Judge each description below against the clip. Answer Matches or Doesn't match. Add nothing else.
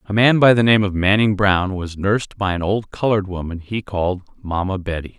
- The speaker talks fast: Matches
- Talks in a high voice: Doesn't match